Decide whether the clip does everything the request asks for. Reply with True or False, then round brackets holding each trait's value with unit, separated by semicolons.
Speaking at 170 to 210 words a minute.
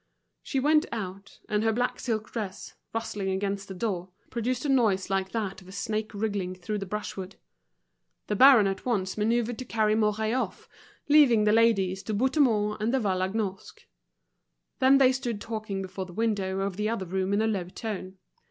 True (180 wpm)